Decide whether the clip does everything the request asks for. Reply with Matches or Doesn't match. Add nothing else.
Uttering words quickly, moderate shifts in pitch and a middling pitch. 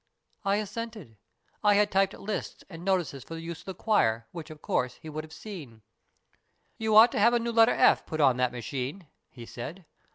Doesn't match